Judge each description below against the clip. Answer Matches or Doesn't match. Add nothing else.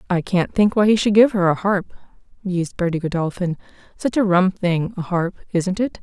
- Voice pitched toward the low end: Doesn't match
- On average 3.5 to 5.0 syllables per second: Doesn't match